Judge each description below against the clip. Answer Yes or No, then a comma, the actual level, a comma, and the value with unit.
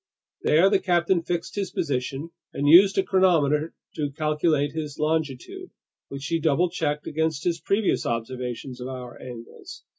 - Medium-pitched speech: Yes, medium, 155 Hz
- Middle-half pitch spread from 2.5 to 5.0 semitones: Yes, average, 3.9 semitones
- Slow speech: No, average, 150 wpm